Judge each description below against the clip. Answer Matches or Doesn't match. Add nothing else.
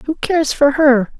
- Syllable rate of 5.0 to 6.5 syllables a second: Doesn't match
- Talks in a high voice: Matches